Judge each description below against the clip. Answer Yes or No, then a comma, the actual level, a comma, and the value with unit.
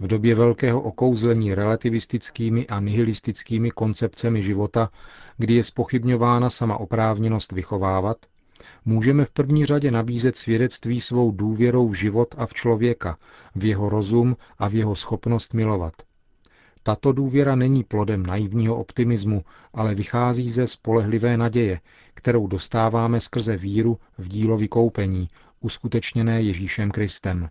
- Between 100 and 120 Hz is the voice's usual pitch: Yes, low, 115 Hz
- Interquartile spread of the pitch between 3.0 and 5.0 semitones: No, narrow, 2.5 semitones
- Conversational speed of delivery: Yes, average, 125 wpm